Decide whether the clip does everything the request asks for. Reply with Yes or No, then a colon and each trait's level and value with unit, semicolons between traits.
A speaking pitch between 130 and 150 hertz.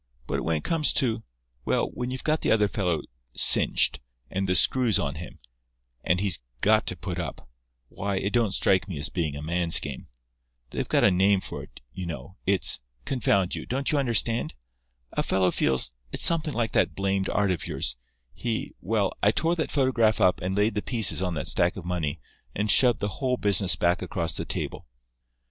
No: very low, 95 Hz